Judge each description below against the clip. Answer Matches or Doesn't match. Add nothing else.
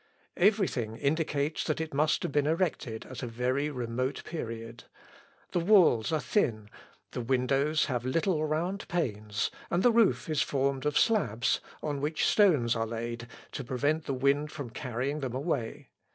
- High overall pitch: Doesn't match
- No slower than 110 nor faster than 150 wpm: Doesn't match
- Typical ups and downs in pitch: Matches